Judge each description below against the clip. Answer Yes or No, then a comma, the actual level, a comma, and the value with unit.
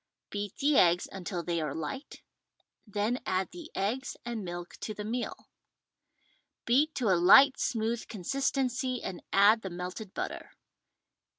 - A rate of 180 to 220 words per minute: No, average, 140 wpm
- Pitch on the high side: Yes, high, 210 Hz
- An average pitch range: No, wide, 5.8 semitones